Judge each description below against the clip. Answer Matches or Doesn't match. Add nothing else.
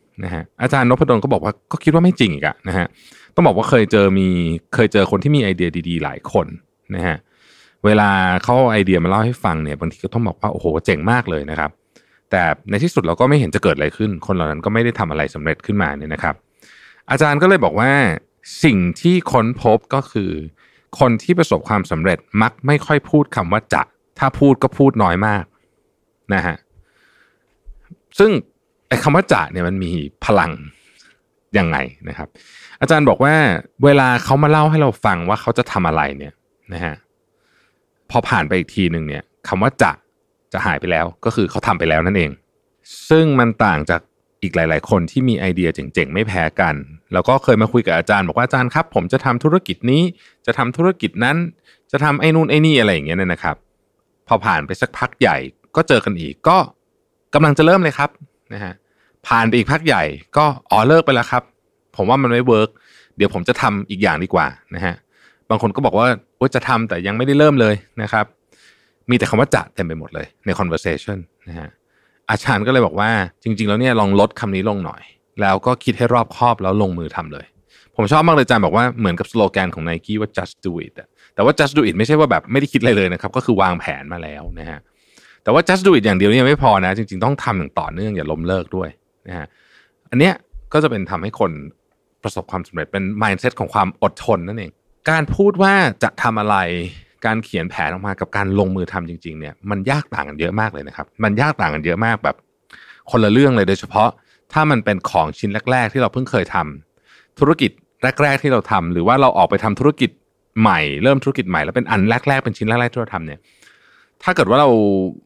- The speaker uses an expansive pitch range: Matches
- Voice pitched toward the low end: Matches